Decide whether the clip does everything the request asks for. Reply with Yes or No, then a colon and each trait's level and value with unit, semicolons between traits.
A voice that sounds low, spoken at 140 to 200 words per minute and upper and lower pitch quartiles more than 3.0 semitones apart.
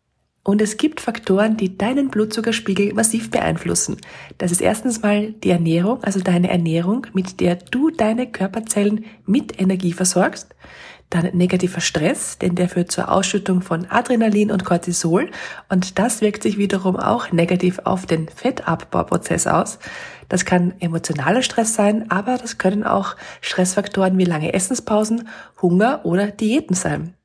No: high, 195 Hz; average, 145 wpm; average, 3.6 semitones